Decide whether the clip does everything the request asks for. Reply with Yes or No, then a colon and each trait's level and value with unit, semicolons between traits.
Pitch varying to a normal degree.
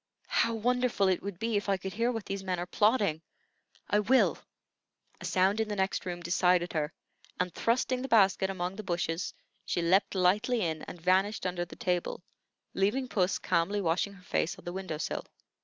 Yes: average, 3.0 semitones